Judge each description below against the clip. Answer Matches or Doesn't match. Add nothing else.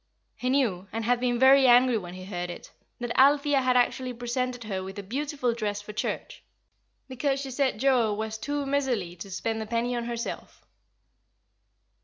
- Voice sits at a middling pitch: Doesn't match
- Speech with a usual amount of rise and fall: Matches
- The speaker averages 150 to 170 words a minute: Doesn't match